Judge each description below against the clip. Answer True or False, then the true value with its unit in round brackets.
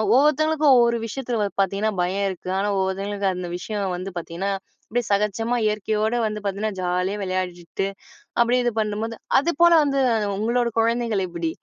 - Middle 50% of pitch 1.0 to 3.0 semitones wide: False (3.7 semitones)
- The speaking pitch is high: True (210 Hz)